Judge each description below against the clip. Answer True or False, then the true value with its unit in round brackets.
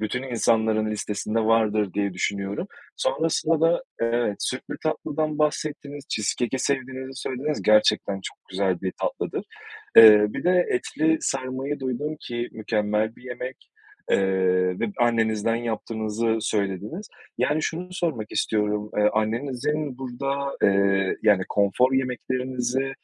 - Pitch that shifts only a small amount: False (4.3 semitones)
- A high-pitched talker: False (120 Hz)